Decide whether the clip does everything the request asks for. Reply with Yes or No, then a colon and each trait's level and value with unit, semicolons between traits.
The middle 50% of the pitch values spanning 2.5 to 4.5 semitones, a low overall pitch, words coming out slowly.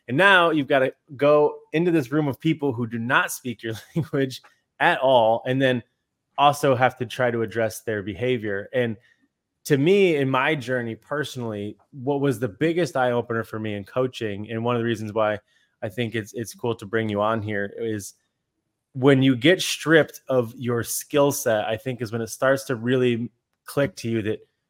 No: average, 3.8 semitones; low, 125 Hz; average, 200 wpm